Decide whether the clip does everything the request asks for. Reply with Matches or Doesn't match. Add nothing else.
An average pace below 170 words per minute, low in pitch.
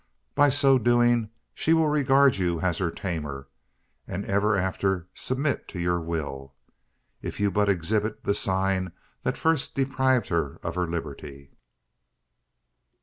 Matches